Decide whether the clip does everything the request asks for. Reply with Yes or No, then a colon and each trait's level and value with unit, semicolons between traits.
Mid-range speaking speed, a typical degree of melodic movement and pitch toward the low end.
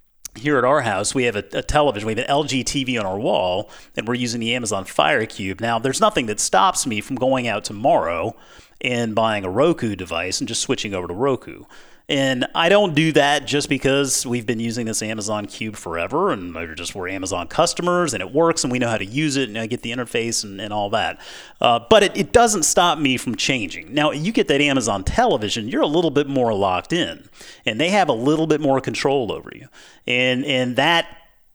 No: fast, 225 wpm; average, 4.7 semitones; low, 125 Hz